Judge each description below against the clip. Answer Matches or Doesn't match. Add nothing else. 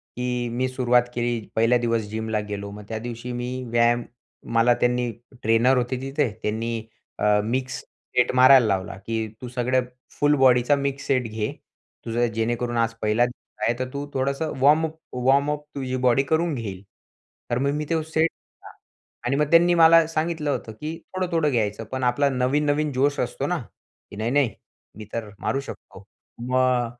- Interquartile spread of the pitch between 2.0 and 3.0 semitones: Doesn't match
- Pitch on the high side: Doesn't match